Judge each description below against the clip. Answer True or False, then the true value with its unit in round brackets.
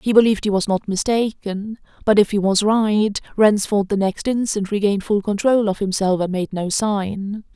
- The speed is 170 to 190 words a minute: True (185 wpm)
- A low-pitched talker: False (205 Hz)